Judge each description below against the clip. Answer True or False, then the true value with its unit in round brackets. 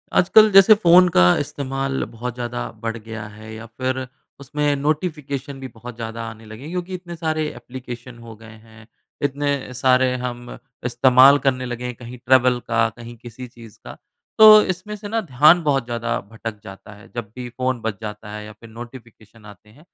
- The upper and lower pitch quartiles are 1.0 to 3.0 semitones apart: False (3.8 semitones)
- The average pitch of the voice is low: True (125 Hz)